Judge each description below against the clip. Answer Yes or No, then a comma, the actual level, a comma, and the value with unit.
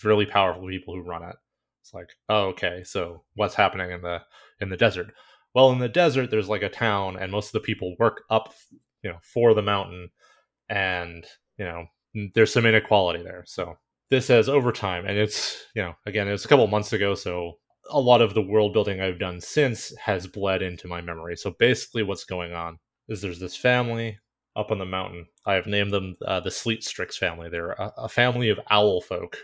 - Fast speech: Yes, fast, 215 wpm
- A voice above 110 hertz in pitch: No, low, 105 Hz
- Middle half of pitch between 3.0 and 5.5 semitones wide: Yes, average, 3.4 semitones